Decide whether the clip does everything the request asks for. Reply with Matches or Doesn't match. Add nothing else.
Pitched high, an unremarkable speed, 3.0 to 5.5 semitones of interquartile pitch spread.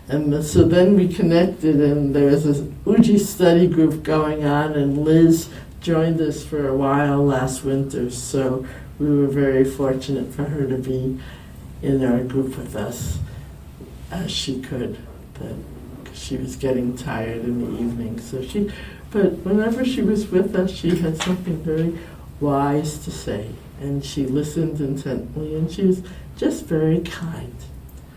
Doesn't match